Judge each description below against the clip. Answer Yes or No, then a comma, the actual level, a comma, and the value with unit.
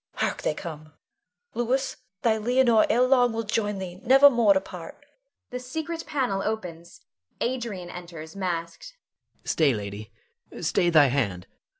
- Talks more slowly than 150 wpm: Yes, average, 140 wpm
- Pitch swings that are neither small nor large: No, wide, 6.8 semitones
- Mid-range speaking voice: No, high, 200 Hz